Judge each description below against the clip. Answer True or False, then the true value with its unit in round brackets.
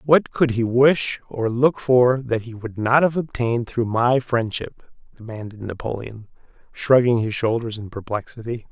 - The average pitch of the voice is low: True (120 Hz)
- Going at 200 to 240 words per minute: False (160 wpm)